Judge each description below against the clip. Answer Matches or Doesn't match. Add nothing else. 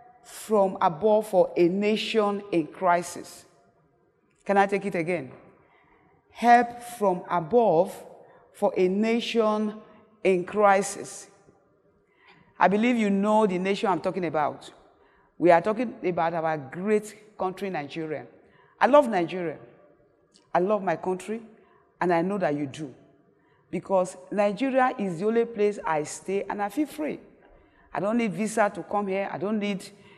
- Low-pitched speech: Doesn't match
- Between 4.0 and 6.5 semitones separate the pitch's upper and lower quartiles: Doesn't match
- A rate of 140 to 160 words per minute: Matches